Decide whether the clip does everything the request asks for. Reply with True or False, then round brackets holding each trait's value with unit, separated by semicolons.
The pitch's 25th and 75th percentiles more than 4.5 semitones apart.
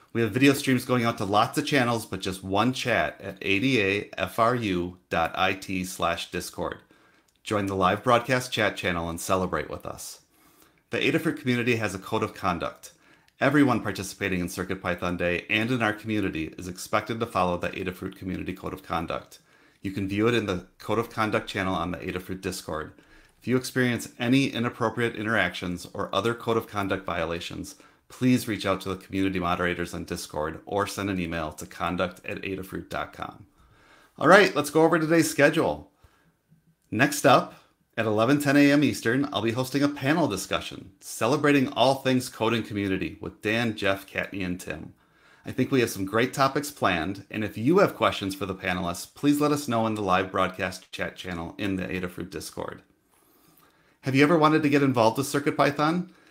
True (5.3 semitones)